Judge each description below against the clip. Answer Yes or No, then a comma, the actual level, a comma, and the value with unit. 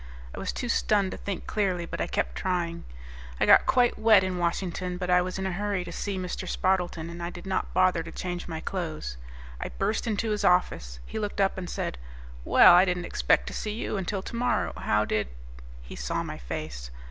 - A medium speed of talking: No, fast, 215 wpm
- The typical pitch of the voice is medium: Yes, medium, 180 Hz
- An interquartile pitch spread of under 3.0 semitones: Yes, narrow, 2.6 semitones